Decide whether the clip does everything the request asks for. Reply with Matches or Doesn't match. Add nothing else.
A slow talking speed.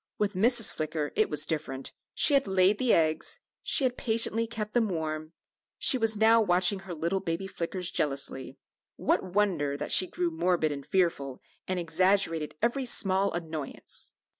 Doesn't match